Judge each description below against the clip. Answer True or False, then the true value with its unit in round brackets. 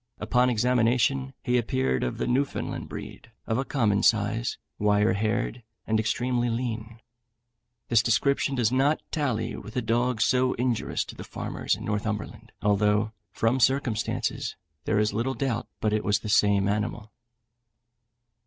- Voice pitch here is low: True (115 Hz)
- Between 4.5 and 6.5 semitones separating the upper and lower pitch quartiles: False (2.9 semitones)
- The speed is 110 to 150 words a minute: True (145 wpm)